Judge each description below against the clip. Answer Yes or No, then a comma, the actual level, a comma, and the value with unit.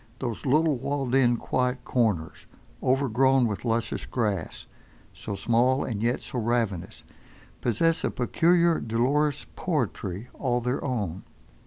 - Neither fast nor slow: No, slow, 125 wpm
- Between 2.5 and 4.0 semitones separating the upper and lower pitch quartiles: Yes, average, 2.9 semitones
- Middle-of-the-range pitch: No, low, 125 Hz